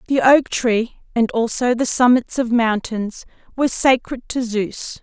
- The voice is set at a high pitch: Yes, high, 235 Hz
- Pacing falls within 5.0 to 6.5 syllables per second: No, 4.1 syllables/s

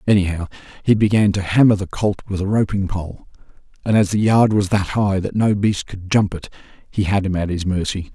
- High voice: No, low, 100 Hz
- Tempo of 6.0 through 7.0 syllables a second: No, 5.5 syllables/s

